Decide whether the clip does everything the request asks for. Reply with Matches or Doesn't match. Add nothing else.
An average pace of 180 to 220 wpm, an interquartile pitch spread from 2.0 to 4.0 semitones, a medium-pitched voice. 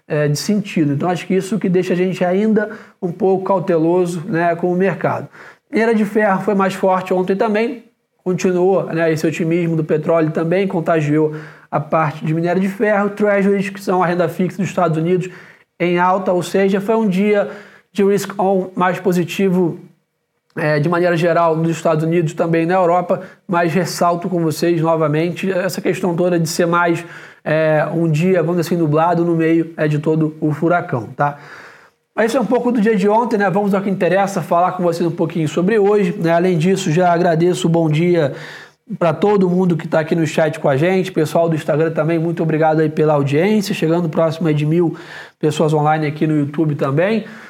Matches